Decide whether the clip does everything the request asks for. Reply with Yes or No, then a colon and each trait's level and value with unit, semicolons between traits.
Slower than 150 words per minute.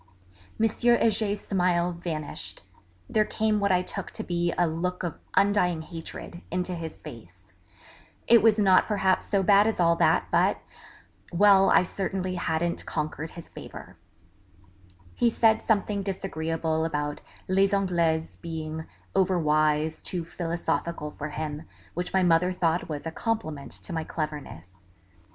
Yes: average, 140 wpm